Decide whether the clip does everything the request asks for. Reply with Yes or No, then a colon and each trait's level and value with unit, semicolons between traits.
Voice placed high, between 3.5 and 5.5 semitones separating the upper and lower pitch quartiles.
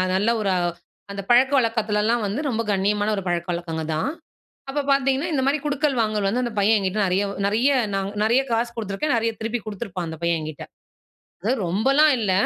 Yes: high, 215 Hz; average, 3.9 semitones